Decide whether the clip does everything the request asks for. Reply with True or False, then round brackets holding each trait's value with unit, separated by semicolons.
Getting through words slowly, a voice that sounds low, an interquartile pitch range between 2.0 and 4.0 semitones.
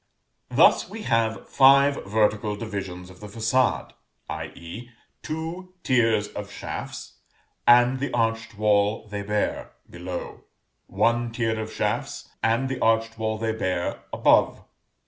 True (125 wpm; 115 Hz; 2.6 semitones)